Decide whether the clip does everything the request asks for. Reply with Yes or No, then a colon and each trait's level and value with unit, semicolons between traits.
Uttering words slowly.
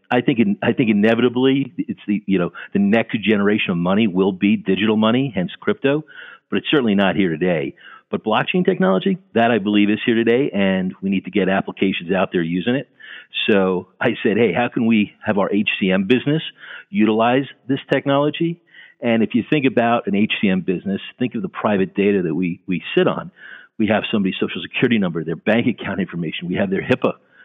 No: average, 200 wpm